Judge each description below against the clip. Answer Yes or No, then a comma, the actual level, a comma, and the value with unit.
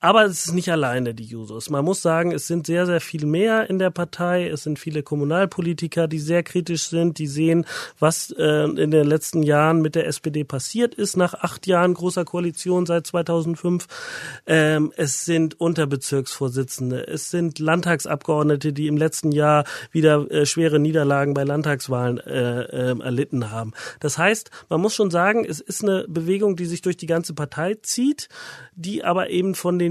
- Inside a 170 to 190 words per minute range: Yes, average, 180 wpm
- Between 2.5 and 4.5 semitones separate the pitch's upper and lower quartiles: Yes, average, 2.9 semitones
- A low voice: No, medium, 165 Hz